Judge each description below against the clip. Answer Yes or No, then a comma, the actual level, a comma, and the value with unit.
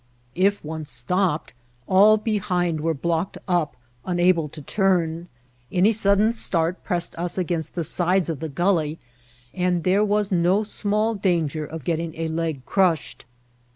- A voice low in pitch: No, medium, 175 Hz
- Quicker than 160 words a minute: No, average, 150 wpm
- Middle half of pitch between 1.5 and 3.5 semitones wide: Yes, average, 3.2 semitones